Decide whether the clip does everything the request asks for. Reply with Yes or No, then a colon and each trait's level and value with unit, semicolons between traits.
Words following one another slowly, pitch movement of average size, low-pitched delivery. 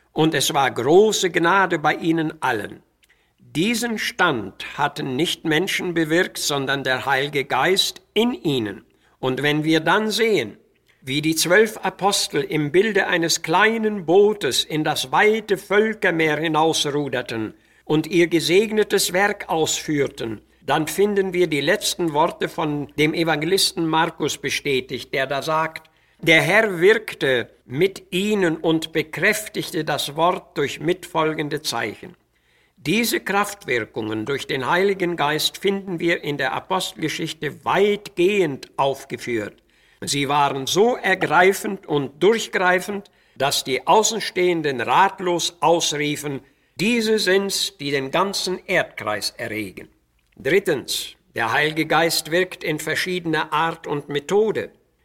No: slow, 120 wpm; average, 4.6 semitones; medium, 165 Hz